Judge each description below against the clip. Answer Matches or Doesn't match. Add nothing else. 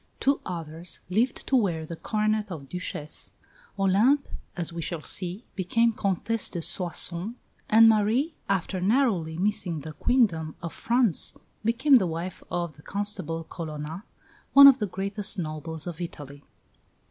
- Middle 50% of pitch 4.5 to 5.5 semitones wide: Matches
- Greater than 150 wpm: Doesn't match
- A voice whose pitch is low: Doesn't match